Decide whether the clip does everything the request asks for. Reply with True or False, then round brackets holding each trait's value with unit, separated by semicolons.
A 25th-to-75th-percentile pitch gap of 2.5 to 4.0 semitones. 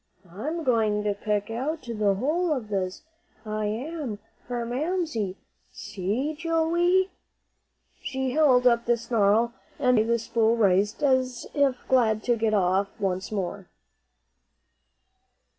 False (4.7 semitones)